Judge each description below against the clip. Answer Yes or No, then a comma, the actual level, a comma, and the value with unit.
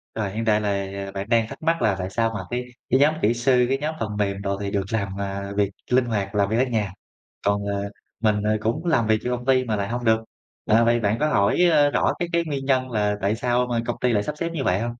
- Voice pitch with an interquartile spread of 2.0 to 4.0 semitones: Yes, average, 3.6 semitones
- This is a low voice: Yes, low, 110 Hz